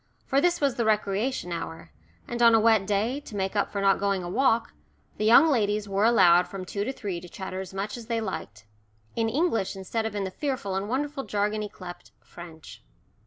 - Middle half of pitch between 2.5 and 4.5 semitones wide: Yes, average, 3.6 semitones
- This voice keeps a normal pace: No, fast, 215 wpm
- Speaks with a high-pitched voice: Yes, high, 210 Hz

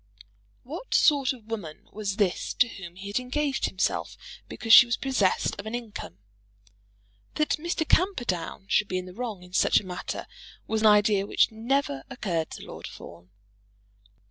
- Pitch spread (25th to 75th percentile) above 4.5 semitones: Yes, average, 5.1 semitones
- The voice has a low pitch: No, high, 215 Hz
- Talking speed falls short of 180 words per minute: Yes, average, 170 wpm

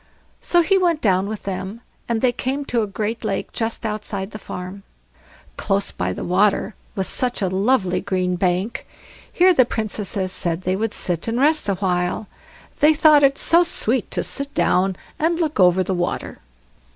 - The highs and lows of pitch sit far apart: Yes, wide, 5.8 semitones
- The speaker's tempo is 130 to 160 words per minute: No, average, 180 wpm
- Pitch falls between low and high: No, high, 210 Hz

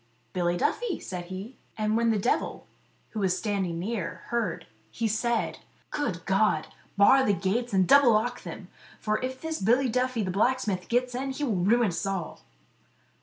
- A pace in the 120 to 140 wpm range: No, average, 170 wpm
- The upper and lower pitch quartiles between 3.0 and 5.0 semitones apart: Yes, average, 4.6 semitones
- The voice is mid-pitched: No, high, 220 Hz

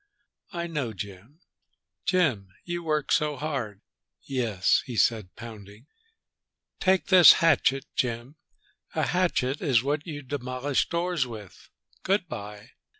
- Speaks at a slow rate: Yes, slow, 120 wpm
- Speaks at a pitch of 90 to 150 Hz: Yes, low, 135 Hz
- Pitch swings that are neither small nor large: No, wide, 6.4 semitones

